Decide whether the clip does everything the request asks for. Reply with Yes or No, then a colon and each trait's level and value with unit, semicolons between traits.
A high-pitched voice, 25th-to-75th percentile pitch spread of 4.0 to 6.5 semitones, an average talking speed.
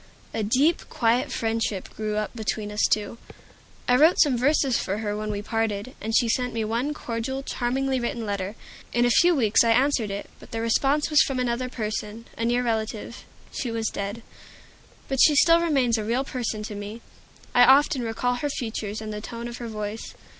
No: high, 230 Hz; average, 2.9 semitones; average, 195 wpm